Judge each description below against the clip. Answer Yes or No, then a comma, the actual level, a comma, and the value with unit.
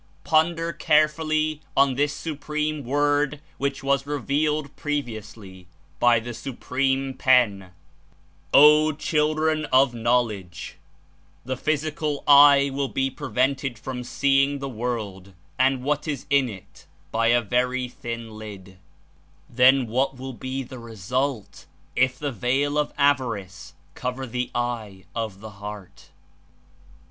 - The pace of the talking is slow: Yes, slow, 125 wpm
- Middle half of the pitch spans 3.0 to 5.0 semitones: Yes, average, 3.6 semitones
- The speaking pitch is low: Yes, low, 130 Hz